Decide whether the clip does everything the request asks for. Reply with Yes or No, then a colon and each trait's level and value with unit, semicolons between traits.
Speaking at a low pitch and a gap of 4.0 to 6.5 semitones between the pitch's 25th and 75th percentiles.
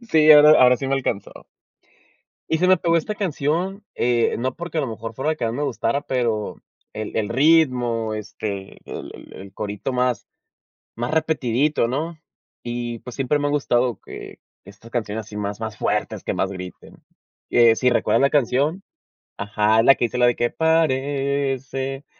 Yes: low, 125 Hz; average, 4.6 semitones